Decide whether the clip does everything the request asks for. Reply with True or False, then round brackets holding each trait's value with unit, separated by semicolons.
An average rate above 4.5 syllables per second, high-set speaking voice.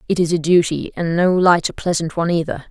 False (6.0 syllables/s; 170 Hz)